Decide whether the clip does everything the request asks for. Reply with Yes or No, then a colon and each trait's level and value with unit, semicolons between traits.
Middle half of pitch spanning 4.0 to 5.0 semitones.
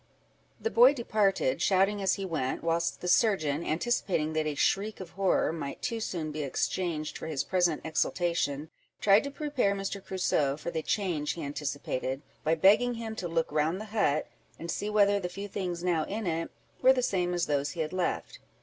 Yes: average, 4.5 semitones